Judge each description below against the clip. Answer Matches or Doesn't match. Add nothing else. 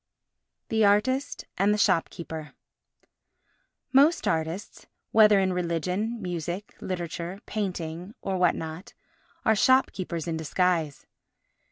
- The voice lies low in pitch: Doesn't match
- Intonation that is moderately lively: Matches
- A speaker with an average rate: Doesn't match